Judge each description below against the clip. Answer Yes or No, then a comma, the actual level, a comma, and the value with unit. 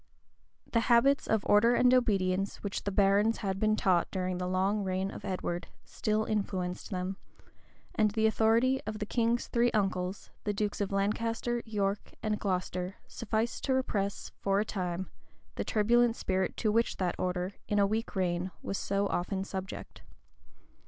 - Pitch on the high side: Yes, high, 200 Hz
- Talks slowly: No, average, 165 wpm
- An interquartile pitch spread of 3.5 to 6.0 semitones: No, average, 2.8 semitones